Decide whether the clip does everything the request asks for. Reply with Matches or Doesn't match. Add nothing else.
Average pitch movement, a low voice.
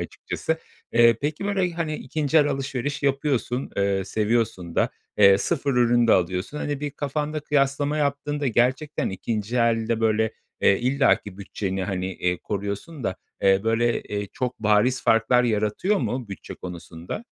Doesn't match